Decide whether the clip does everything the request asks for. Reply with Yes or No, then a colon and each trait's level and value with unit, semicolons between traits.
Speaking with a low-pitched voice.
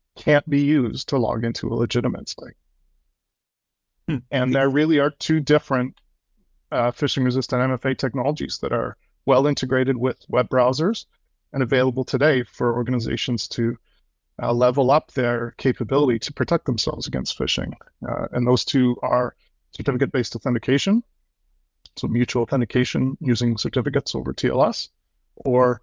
Yes: low, 125 Hz